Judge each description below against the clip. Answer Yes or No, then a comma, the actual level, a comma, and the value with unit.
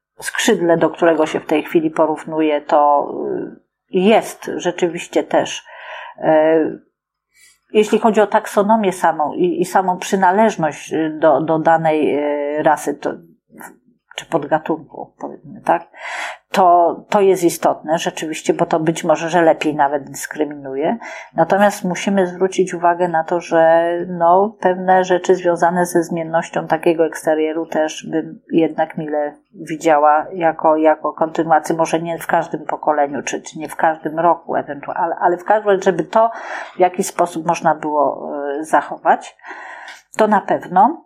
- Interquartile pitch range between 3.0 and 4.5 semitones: No, narrow, 2.5 semitones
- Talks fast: No, average, 135 wpm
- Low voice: No, medium, 165 Hz